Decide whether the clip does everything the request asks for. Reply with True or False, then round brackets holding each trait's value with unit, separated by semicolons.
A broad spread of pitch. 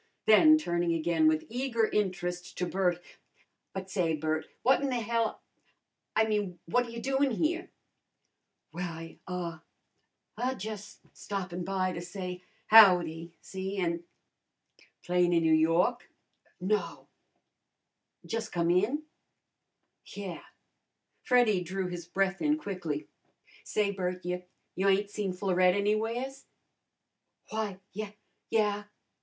False (3.7 semitones)